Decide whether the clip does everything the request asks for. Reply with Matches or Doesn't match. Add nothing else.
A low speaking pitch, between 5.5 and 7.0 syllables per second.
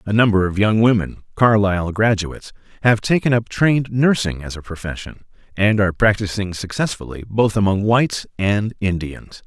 Doesn't match